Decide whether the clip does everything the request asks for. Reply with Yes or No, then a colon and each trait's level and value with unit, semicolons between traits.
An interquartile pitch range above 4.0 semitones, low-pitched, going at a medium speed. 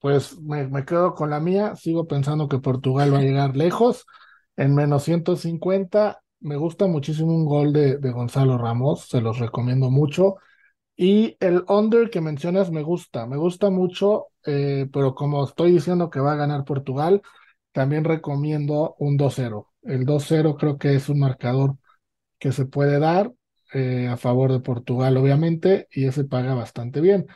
No: average, 4.4 semitones; medium, 145 Hz; average, 170 wpm